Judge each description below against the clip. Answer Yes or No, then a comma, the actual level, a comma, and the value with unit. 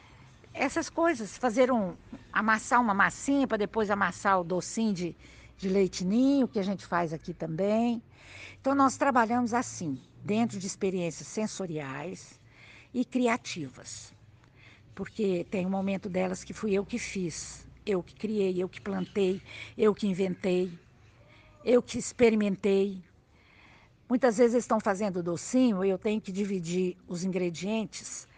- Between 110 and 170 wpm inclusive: Yes, average, 140 wpm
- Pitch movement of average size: Yes, average, 4.4 semitones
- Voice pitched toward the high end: Yes, high, 195 Hz